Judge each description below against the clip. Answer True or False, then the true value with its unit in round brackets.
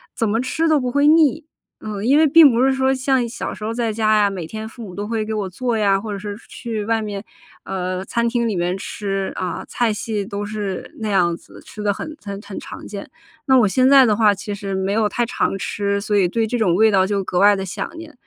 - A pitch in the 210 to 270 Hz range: True (215 Hz)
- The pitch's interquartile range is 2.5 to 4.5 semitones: True (3.3 semitones)